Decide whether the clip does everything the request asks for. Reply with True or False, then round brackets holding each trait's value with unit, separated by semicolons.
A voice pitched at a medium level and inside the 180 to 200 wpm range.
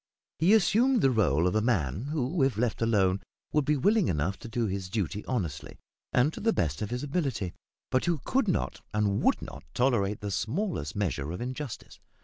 False (115 Hz; 195 wpm)